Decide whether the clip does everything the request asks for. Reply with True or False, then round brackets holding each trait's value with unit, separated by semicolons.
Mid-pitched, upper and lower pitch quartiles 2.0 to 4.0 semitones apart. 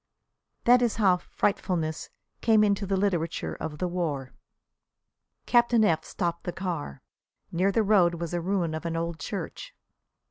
True (180 Hz; 3.5 semitones)